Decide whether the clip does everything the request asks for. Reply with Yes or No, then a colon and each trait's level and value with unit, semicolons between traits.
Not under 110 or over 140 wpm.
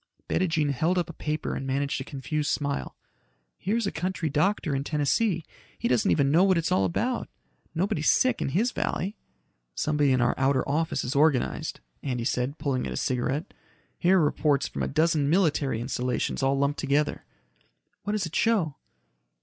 No: average, 175 wpm